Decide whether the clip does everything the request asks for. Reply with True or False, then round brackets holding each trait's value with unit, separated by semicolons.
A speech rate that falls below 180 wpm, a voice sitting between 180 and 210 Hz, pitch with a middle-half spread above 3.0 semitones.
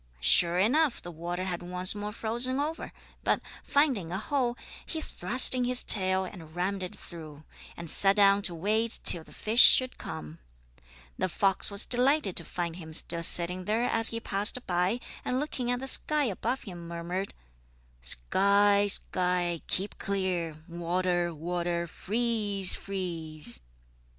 True (155 wpm; 190 Hz; 4.7 semitones)